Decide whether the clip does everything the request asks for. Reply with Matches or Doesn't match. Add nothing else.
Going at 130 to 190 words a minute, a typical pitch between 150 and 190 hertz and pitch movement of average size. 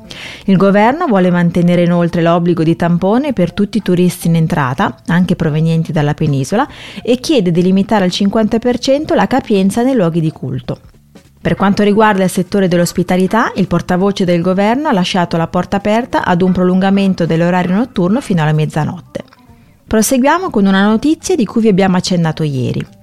Matches